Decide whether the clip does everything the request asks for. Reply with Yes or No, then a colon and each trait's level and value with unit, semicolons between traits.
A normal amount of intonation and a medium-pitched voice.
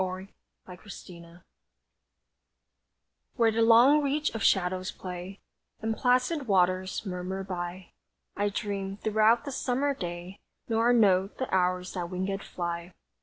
No: average, 3.9 semitones; high, 195 Hz